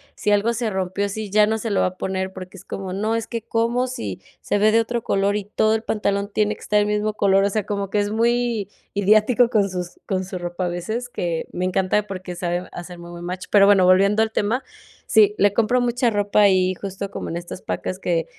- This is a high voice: Yes, high, 200 Hz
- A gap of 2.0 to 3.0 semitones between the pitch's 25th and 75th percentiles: Yes, narrow, 2.6 semitones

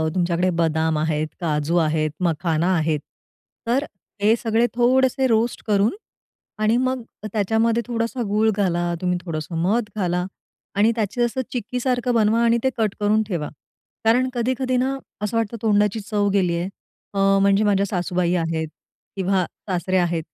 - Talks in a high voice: Yes, high, 205 Hz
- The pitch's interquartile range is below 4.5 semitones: No, average, 5.0 semitones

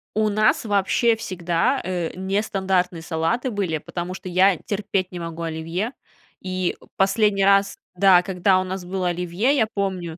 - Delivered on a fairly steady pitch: Yes, narrow, 2.3 semitones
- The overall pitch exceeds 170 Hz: Yes, high, 190 Hz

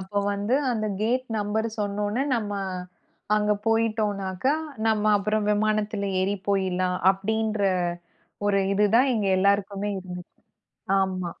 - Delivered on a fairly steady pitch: Yes, narrow, 1.8 semitones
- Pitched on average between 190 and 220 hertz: Yes, high, 205 Hz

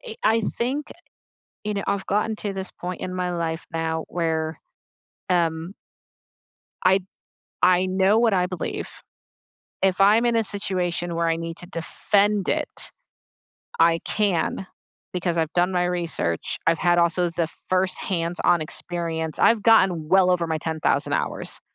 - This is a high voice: No, medium, 180 Hz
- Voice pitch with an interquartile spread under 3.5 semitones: Yes, average, 2.8 semitones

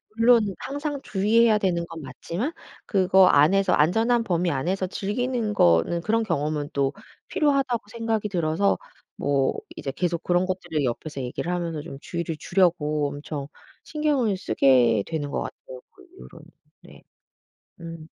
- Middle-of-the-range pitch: Yes, medium, 175 Hz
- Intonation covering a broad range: Yes, wide, 6.8 semitones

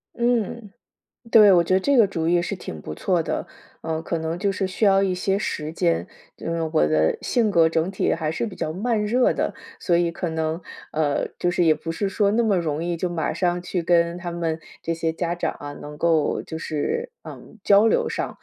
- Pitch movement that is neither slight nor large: Yes, average, 3.5 semitones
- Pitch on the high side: No, medium, 175 Hz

